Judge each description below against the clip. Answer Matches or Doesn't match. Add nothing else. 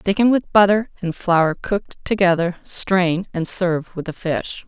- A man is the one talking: Doesn't match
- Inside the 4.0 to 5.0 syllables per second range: Matches